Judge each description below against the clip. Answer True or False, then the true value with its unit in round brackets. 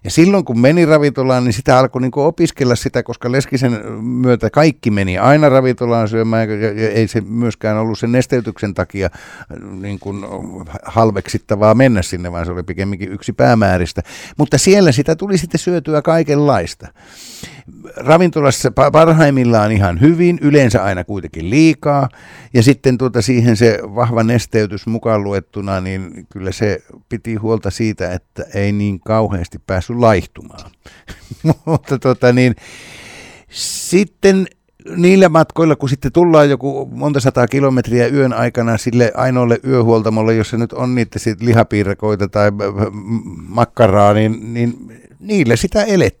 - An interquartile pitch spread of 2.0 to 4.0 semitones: False (4.6 semitones)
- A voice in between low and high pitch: False (120 Hz)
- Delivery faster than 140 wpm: False (135 wpm)